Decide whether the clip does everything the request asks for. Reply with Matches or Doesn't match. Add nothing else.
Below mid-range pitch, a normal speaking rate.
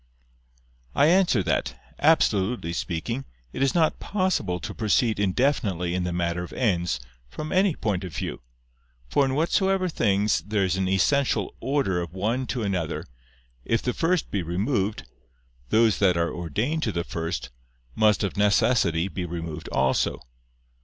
Matches